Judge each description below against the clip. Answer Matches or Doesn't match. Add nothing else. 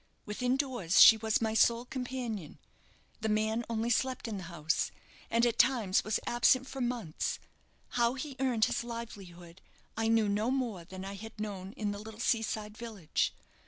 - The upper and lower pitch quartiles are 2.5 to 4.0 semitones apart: Matches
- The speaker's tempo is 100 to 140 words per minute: Doesn't match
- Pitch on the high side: Matches